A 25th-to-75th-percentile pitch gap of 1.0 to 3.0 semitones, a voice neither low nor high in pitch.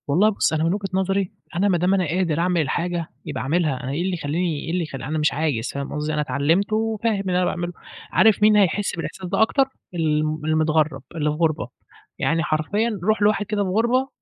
No: average, 4.5 semitones; medium, 175 Hz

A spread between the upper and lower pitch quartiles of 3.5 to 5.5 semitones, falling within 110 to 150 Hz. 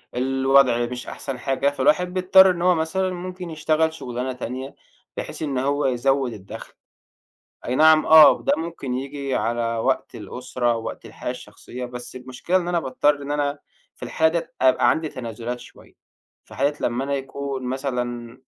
Yes: average, 4.0 semitones; low, 135 Hz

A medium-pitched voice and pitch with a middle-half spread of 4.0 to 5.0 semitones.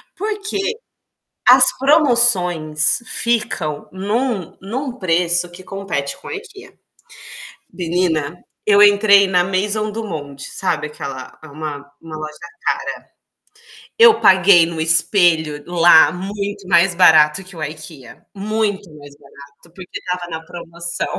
Yes: medium, 180 Hz; average, 4.4 semitones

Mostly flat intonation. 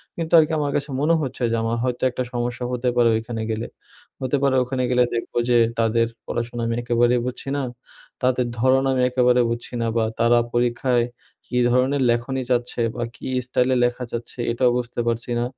Yes: narrow, 1.4 semitones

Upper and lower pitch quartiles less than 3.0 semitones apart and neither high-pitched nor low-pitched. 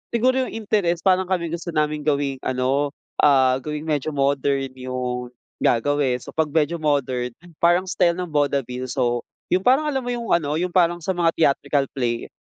No: average, 4.7 semitones; medium, 150 Hz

